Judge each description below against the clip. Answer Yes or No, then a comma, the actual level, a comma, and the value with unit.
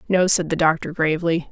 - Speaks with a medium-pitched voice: Yes, medium, 165 Hz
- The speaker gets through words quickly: No, average, 195 wpm